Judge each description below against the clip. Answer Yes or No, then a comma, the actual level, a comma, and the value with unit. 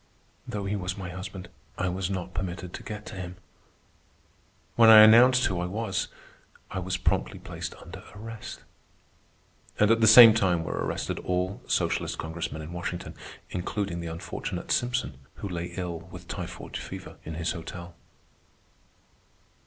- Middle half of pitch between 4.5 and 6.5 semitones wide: No, average, 3.2 semitones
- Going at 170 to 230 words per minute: No, average, 155 wpm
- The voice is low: Yes, very low, 95 Hz